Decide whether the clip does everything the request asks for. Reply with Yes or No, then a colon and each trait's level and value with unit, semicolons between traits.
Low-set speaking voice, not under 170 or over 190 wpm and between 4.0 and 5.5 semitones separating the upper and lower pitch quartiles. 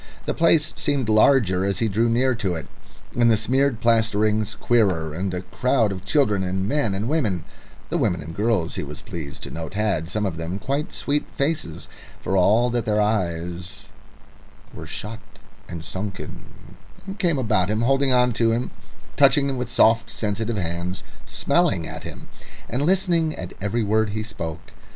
Yes: low, 110 Hz; average, 175 wpm; average, 4.7 semitones